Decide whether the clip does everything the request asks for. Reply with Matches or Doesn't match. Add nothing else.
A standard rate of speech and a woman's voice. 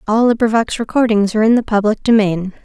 Matches